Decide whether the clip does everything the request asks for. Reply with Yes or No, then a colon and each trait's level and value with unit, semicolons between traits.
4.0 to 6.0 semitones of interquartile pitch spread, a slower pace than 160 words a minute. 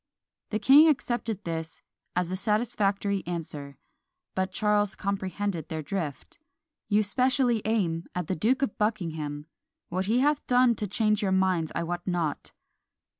Yes: average, 4.3 semitones; average, 145 wpm